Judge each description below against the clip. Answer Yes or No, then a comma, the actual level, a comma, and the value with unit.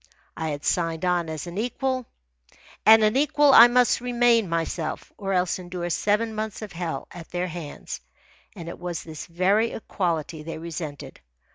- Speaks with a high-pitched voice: No, medium, 180 Hz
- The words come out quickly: No, average, 165 wpm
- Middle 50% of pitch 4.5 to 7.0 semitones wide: Yes, average, 5.0 semitones